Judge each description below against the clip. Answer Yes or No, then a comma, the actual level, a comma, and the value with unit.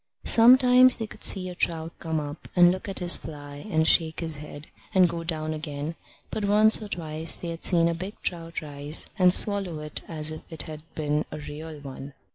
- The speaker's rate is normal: No, fast, 215 wpm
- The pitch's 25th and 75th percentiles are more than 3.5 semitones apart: No, average, 3.2 semitones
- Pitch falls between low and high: Yes, medium, 165 Hz